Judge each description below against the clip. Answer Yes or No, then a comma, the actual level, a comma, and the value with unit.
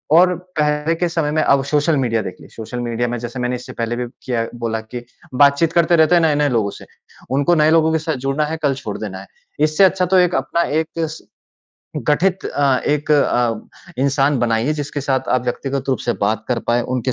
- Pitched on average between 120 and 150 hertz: Yes, medium, 140 Hz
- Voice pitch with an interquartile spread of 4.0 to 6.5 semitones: Yes, average, 4.3 semitones